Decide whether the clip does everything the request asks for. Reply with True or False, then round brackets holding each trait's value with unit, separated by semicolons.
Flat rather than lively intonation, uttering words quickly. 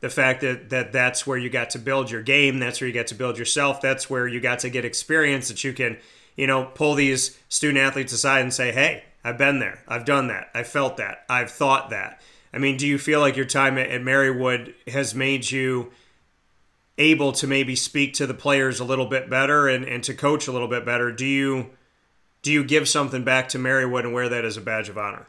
True (1.7 semitones; 235 wpm)